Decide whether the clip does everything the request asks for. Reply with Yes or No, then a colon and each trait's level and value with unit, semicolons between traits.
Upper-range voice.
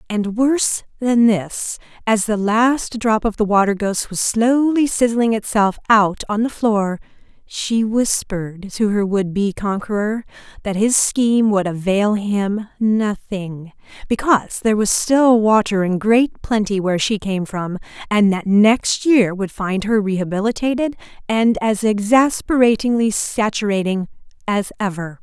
Yes: high, 210 Hz